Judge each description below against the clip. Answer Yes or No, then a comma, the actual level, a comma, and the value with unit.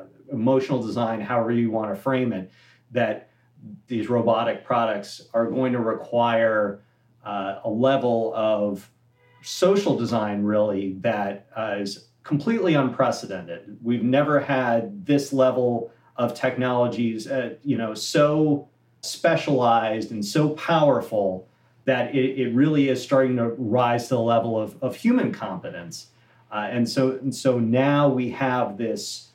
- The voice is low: Yes, low, 120 Hz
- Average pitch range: Yes, average, 3.0 semitones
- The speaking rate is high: No, slow, 135 wpm